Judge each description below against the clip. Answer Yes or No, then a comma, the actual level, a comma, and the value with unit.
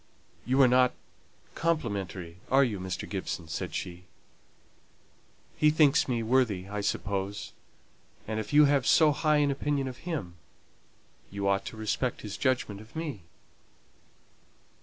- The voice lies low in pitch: Yes, low, 120 Hz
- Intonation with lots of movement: Yes, wide, 6.3 semitones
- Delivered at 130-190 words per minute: Yes, average, 140 wpm